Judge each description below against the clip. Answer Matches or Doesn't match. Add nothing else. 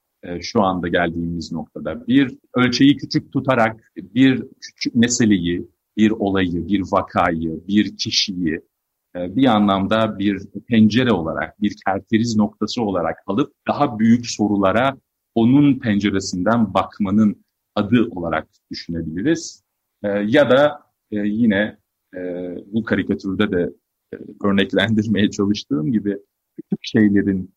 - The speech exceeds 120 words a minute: Doesn't match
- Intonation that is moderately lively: Matches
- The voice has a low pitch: Matches